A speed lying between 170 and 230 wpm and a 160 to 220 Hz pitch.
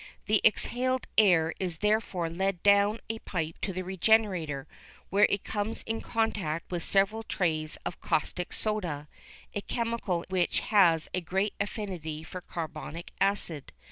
No: average, 140 wpm; high, 190 Hz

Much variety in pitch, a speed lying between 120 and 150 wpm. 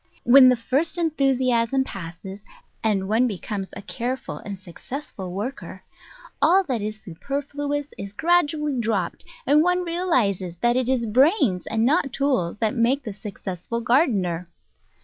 Yes: wide, 5.9 semitones; average, 145 wpm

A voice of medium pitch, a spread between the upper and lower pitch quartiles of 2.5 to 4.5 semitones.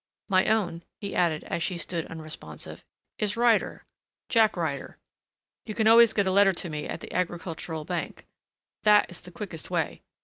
Yes: medium, 180 Hz; average, 4.0 semitones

